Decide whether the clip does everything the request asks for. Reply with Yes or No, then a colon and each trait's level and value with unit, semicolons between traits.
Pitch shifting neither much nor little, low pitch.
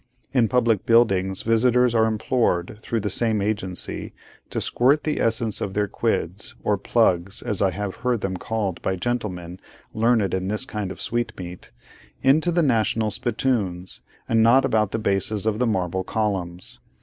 Yes: average, 3.6 semitones; low, 110 Hz